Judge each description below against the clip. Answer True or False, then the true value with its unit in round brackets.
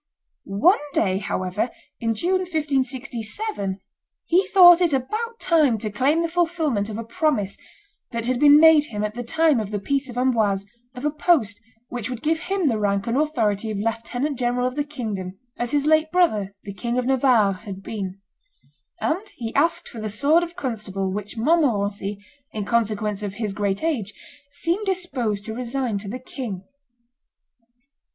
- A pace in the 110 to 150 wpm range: False (175 wpm)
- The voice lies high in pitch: True (245 Hz)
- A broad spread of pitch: True (6.7 semitones)